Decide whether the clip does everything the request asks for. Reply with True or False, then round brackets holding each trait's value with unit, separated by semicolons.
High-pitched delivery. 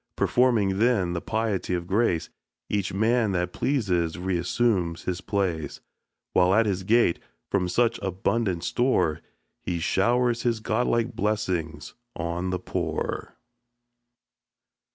False (95 Hz)